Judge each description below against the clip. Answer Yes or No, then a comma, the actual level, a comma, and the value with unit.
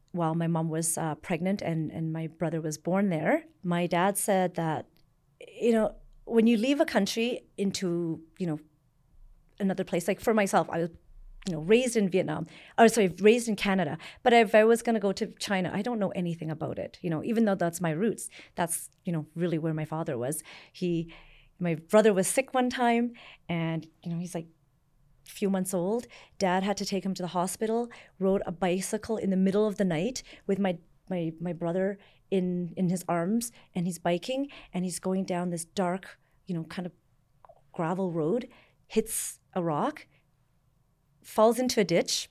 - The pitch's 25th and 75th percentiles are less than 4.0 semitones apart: No, average, 4.3 semitones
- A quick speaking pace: No, average, 195 wpm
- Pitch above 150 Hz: Yes, medium, 185 Hz